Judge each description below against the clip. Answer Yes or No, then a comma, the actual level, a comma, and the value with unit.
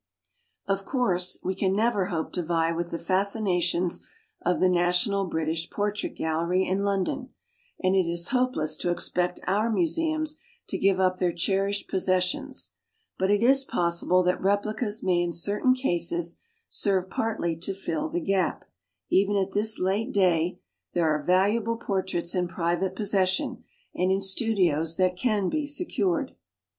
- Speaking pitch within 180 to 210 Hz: Yes, high, 190 Hz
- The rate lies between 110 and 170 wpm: Yes, average, 160 wpm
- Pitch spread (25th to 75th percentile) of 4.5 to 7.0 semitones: No, average, 2.8 semitones